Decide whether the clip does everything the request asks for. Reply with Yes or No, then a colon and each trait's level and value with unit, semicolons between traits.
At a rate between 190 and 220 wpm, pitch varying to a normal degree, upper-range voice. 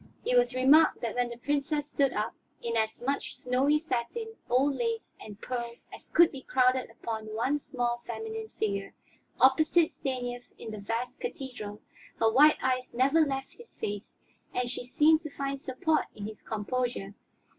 No: average, 165 wpm; average, 3.7 semitones; very high, 255 Hz